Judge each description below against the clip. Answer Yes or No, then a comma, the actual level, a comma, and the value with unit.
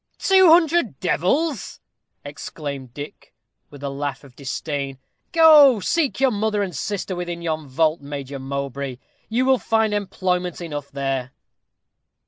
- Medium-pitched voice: Yes, medium, 170 Hz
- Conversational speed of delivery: No, slow, 130 wpm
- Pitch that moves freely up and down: Yes, wide, 8.1 semitones